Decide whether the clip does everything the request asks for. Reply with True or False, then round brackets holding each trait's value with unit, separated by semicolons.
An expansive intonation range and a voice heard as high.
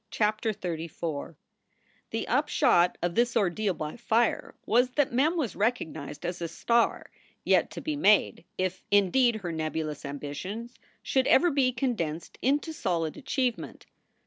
True (6.7 semitones; 210 Hz)